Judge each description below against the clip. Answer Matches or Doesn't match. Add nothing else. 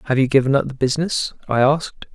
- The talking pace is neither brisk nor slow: Doesn't match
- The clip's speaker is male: Matches